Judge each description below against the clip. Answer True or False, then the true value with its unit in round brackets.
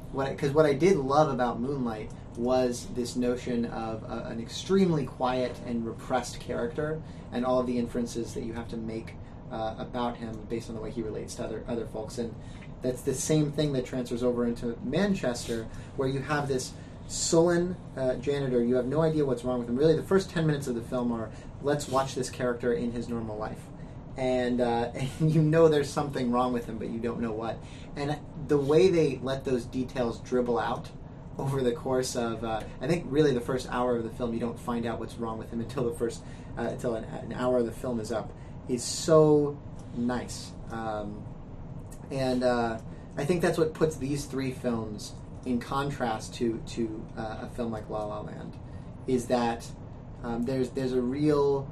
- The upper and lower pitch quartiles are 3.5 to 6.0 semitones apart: False (2.9 semitones)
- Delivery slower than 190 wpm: False (200 wpm)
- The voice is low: True (125 Hz)